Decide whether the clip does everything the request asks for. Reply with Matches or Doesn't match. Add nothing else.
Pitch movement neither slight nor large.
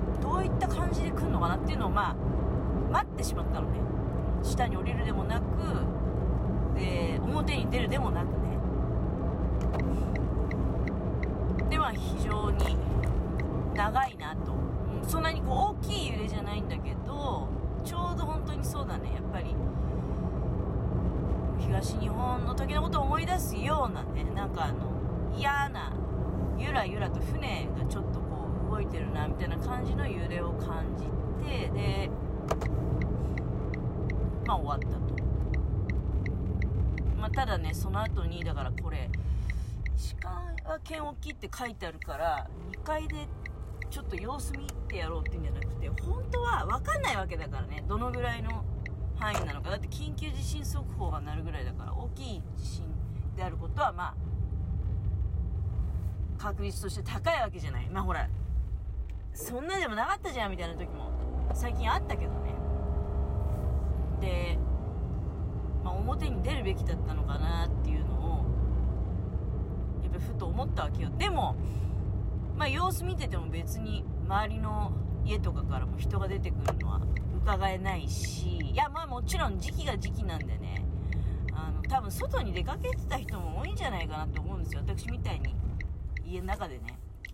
Doesn't match